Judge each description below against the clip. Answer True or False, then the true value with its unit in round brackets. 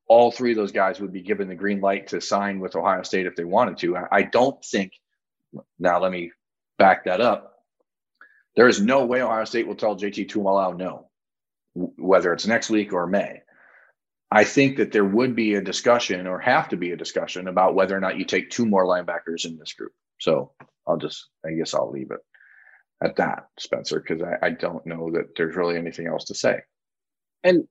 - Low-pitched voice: True (95 Hz)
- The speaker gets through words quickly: True (210 wpm)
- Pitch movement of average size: True (3.5 semitones)